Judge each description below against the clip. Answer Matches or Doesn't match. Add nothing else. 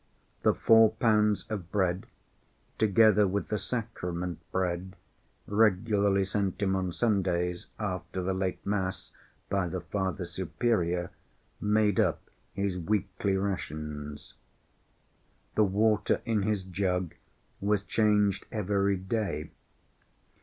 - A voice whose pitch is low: Matches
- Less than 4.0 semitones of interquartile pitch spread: Matches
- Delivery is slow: Matches